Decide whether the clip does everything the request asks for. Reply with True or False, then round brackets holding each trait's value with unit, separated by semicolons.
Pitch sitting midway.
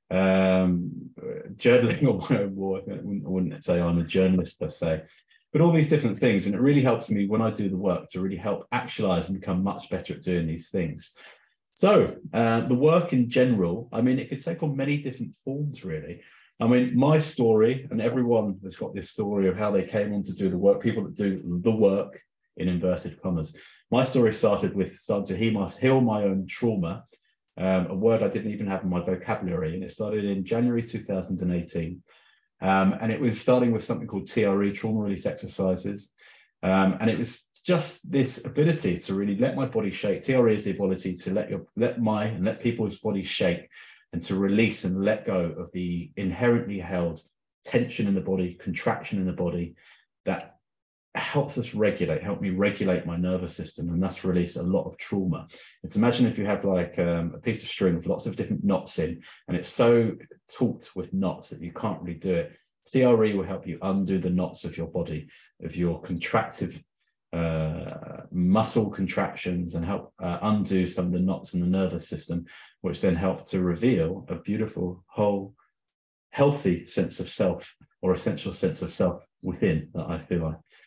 False (100 Hz)